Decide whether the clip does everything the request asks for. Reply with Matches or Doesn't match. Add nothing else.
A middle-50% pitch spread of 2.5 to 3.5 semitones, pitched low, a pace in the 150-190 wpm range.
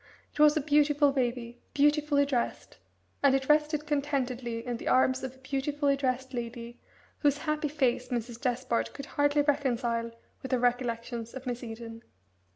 Doesn't match